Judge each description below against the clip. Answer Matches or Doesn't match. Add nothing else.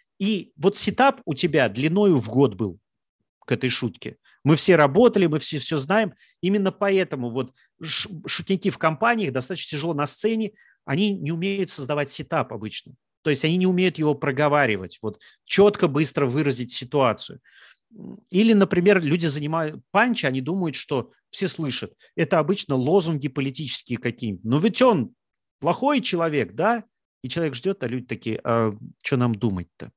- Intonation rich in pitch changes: Matches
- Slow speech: Doesn't match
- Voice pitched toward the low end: Doesn't match